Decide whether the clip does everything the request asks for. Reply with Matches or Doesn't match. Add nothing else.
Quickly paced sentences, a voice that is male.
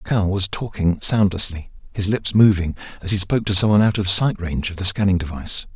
Matches